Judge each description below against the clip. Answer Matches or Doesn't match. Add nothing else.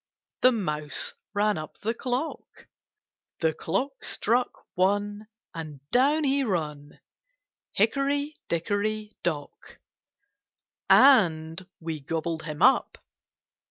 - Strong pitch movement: Matches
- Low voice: Doesn't match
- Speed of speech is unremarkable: Doesn't match